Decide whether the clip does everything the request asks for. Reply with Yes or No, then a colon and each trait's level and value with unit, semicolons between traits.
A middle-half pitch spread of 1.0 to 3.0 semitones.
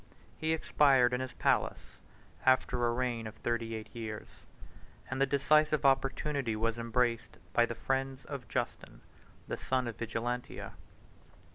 Yes: narrow, 2.6 semitones